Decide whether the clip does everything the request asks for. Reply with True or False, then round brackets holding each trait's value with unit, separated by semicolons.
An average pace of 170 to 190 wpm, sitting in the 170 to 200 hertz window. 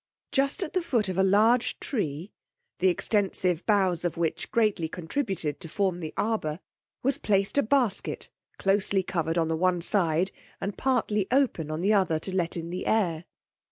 True (175 wpm; 190 Hz)